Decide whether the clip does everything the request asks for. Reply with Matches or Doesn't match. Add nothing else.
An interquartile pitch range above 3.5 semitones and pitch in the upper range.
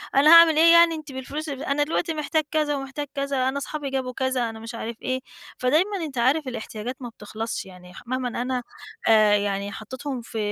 Matches